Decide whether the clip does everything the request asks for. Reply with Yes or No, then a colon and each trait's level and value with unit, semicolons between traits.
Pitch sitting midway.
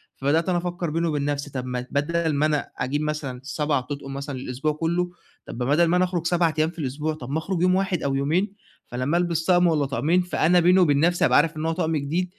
Yes: medium, 155 Hz